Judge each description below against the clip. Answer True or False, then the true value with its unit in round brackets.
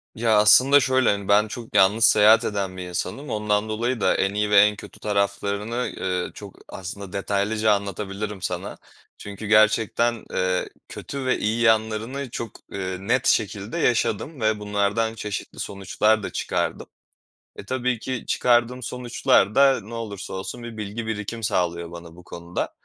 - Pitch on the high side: False (105 Hz)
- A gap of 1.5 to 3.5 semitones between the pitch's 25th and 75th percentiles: True (2.7 semitones)